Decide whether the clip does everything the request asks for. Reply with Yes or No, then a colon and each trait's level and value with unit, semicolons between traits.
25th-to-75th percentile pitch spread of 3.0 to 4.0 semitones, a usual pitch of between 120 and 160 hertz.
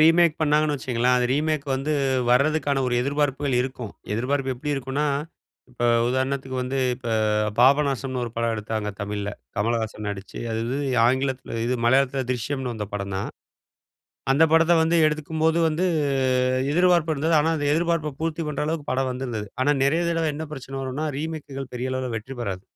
Yes: average, 3.6 semitones; low, 135 Hz